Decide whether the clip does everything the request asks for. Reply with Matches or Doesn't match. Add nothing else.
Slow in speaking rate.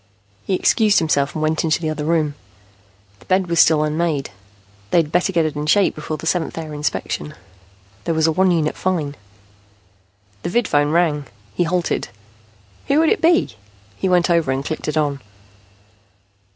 Doesn't match